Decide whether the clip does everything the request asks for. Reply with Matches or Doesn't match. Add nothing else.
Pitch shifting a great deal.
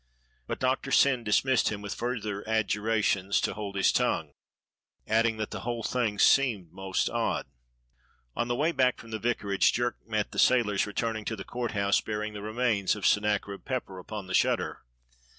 Doesn't match